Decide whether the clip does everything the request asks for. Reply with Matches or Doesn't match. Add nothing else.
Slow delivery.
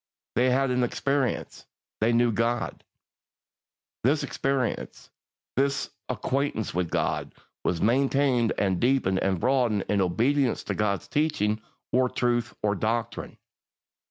Matches